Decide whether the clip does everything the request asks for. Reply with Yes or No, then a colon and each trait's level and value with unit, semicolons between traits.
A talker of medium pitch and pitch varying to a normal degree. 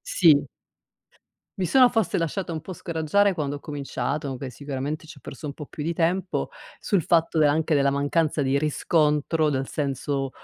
Yes: medium, 150 Hz; average, 3.0 semitones